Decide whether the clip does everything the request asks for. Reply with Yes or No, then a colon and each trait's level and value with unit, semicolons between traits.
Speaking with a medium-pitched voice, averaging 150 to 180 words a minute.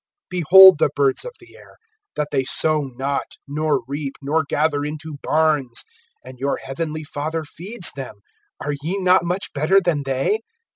Yes: medium, 150 Hz; average, 160 wpm